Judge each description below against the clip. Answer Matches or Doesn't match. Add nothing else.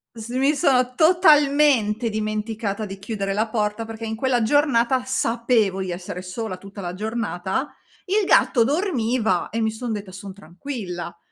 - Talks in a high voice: Matches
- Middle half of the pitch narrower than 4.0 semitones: Doesn't match